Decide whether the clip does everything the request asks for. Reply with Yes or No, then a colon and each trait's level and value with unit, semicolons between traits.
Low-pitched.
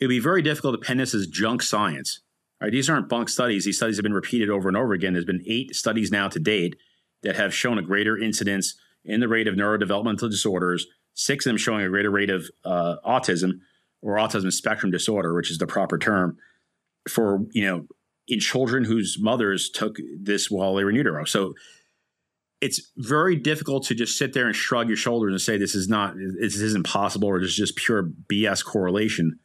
Yes: low, 105 Hz